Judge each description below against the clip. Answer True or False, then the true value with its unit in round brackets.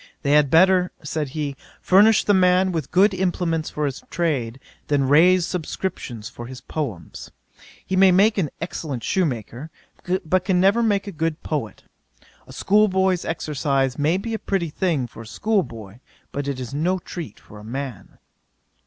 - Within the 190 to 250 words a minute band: False (170 wpm)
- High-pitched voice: False (160 Hz)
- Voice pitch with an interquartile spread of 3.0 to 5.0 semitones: False (5.5 semitones)